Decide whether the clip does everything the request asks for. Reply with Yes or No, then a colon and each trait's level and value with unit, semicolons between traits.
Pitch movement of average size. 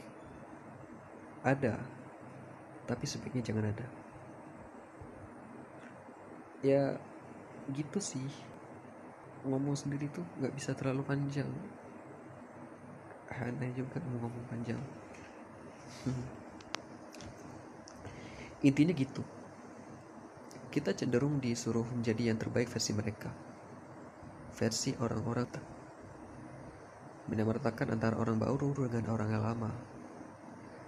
Yes: average, 3.2 semitones